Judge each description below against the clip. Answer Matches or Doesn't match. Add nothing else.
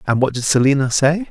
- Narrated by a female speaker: Doesn't match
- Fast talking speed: Matches